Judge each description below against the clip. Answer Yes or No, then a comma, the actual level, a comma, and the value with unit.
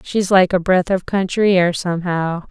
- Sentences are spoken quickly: No, average, 190 wpm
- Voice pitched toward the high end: No, medium, 180 Hz